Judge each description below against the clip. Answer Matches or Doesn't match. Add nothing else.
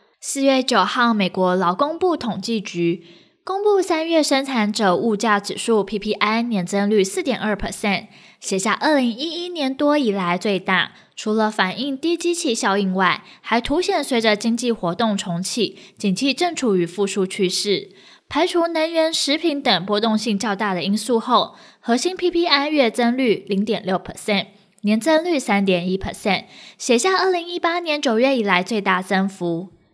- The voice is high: Matches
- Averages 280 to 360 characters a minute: Matches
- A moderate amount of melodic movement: Doesn't match